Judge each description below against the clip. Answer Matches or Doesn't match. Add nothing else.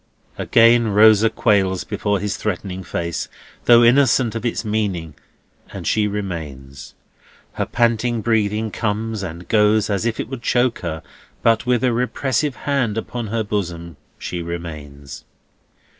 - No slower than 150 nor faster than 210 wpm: Doesn't match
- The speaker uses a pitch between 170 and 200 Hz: Doesn't match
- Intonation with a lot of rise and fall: Doesn't match